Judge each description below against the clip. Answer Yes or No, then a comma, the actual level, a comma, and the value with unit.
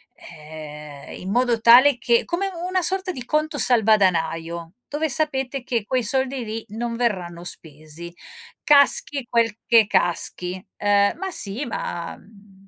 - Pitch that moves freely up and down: Yes, wide, 6.9 semitones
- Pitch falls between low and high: No, high, 225 Hz